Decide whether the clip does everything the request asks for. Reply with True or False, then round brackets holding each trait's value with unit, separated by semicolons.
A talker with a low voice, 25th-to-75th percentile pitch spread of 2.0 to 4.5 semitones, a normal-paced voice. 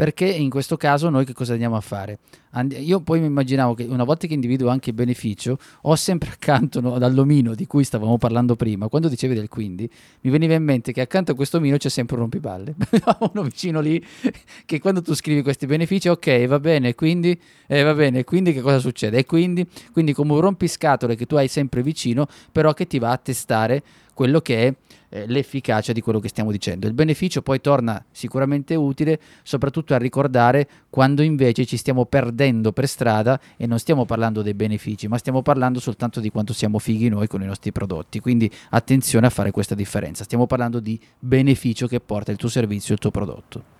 False (130 Hz; 4.1 semitones; 205 wpm)